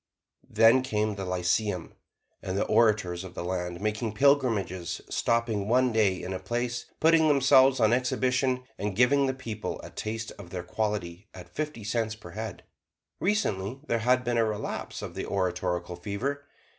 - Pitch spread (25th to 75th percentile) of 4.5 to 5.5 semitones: Yes, average, 5.2 semitones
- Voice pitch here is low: Yes, low, 110 Hz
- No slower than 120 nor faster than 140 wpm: No, average, 165 wpm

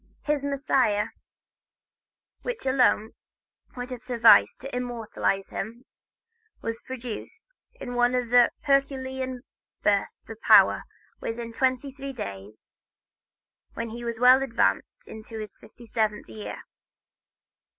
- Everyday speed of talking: No, slow, 115 wpm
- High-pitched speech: Yes, high, 245 Hz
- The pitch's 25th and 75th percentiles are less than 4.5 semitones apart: Yes, average, 2.7 semitones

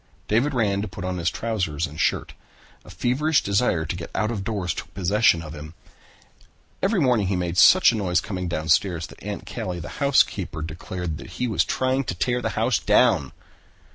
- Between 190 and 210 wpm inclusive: Yes, average, 195 wpm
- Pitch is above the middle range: No, very low, 95 Hz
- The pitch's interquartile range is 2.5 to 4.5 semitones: No, average, 5.2 semitones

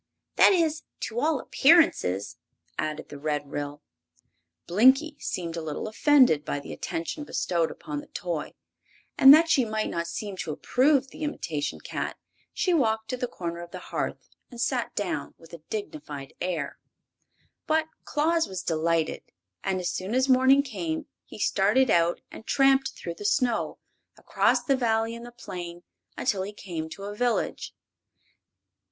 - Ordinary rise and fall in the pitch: No, wide, 7.9 semitones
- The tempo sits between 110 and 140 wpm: No, average, 160 wpm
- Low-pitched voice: No, high, 205 Hz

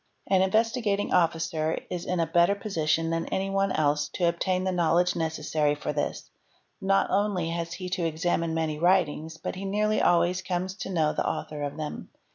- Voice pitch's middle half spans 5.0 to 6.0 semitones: No, average, 2.9 semitones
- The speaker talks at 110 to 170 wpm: No, average, 185 wpm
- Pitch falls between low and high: Yes, medium, 170 Hz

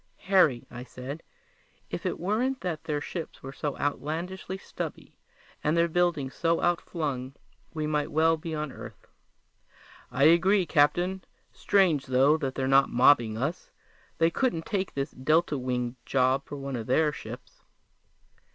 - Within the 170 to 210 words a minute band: No, average, 150 wpm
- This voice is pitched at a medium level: Yes, medium, 150 Hz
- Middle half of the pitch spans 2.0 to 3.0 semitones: No, average, 4.1 semitones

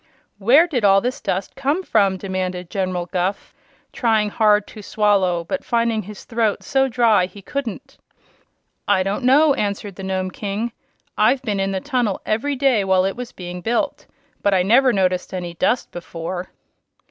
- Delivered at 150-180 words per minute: Yes, average, 170 wpm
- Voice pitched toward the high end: Yes, high, 205 Hz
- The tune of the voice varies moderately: Yes, average, 4.3 semitones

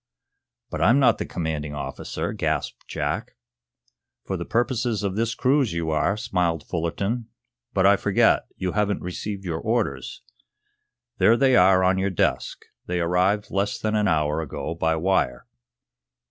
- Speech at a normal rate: Yes, average, 150 wpm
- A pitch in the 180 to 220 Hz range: No, very low, 95 Hz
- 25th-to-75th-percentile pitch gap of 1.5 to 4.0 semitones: No, average, 4.7 semitones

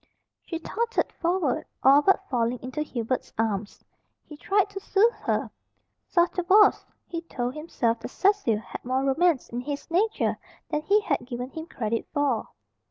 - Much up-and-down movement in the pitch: Yes, wide, 6.8 semitones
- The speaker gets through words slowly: No, average, 160 wpm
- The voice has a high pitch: Yes, very high, 295 Hz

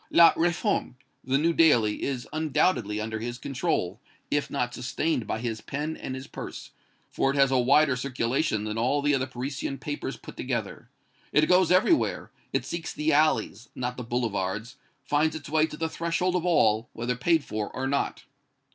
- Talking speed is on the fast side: No, average, 180 wpm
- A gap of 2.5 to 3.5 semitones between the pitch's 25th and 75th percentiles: No, average, 4.5 semitones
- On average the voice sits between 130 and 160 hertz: Yes, low, 135 Hz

